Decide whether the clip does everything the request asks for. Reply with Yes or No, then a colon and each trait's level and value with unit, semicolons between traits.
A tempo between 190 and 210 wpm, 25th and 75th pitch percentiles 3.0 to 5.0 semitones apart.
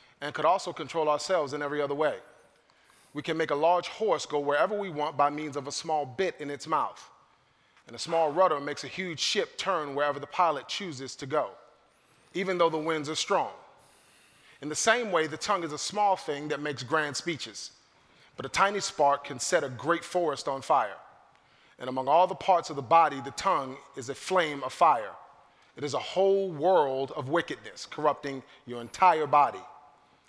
Yes: average, 200 wpm; average, 3.5 semitones